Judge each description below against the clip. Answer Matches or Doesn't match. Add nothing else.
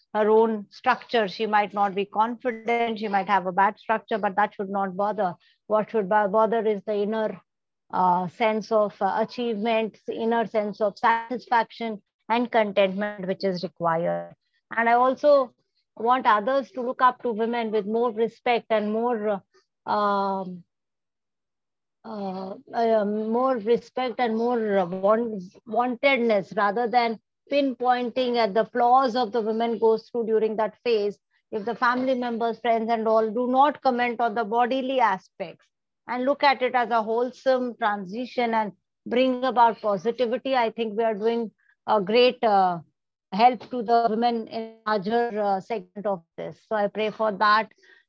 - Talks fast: Doesn't match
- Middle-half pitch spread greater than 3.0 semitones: Doesn't match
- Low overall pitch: Doesn't match